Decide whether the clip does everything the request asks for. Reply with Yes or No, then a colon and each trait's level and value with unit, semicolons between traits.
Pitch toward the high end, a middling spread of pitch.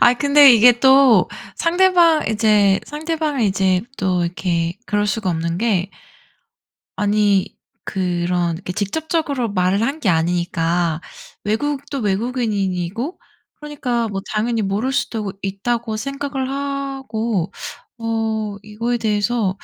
No: high, 220 Hz; wide, 5.8 semitones